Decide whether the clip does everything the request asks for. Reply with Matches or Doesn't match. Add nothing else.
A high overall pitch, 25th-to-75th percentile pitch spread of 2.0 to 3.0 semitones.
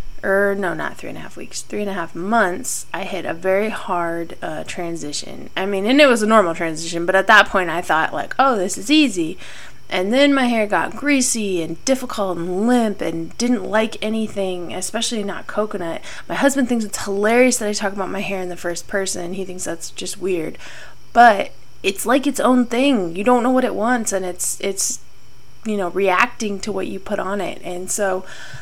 Doesn't match